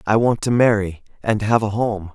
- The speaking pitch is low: Yes, low, 105 Hz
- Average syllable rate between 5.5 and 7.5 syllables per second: No, 4.9 syllables/s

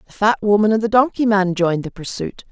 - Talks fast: Yes, fast, 240 wpm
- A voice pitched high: Yes, high, 205 Hz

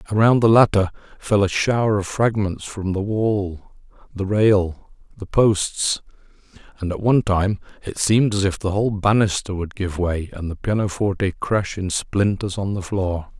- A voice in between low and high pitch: No, low, 100 Hz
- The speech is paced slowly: No, average, 170 wpm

